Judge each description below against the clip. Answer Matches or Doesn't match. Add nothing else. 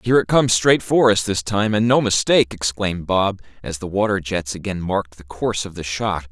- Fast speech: Matches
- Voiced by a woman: Doesn't match